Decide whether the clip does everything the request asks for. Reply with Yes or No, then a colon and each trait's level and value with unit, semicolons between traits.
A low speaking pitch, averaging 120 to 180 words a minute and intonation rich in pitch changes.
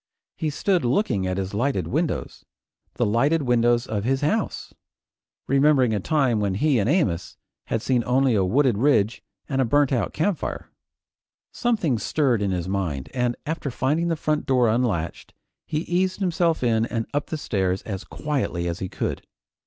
Yes: low, 125 Hz; average, 170 wpm; wide, 6.4 semitones